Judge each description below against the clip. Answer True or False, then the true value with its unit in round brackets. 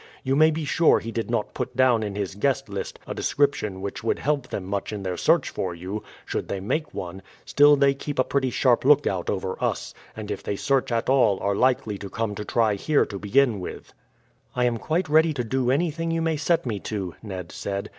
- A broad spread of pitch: True (5.9 semitones)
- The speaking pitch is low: True (120 Hz)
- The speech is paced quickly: True (225 wpm)